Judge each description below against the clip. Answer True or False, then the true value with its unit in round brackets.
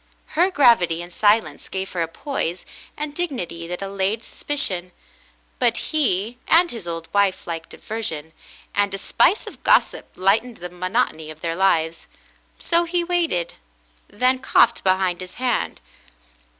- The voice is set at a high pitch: True (195 Hz)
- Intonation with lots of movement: True (6.5 semitones)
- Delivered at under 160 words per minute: True (150 wpm)